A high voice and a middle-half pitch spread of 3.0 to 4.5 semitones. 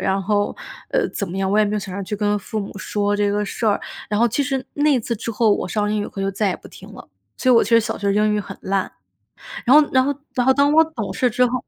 Yes: high, 210 Hz; average, 3.5 semitones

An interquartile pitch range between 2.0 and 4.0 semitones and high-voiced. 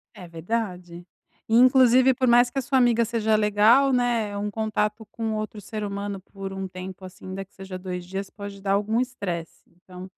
Yes: average, 3.4 semitones; high, 205 Hz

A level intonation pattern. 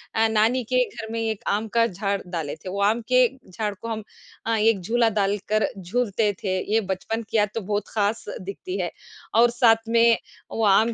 Yes: narrow, 2.3 semitones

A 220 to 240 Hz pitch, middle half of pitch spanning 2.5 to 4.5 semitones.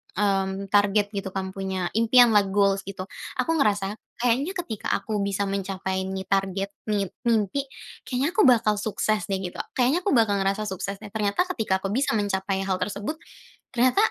No: high, 205 Hz; average, 2.8 semitones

